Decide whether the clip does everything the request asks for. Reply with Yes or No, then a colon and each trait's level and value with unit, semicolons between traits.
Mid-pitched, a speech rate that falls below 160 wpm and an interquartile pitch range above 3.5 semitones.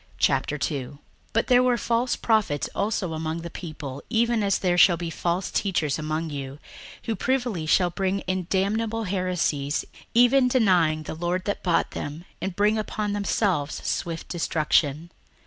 Yes: medium, 180 Hz; average, 150 wpm; average, 5.2 semitones